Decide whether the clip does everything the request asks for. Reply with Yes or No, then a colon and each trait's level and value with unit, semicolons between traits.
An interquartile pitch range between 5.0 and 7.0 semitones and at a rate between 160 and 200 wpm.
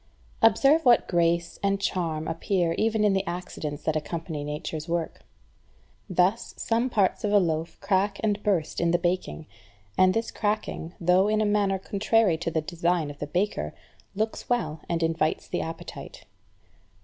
No: average, 4.0 semitones; average, 165 wpm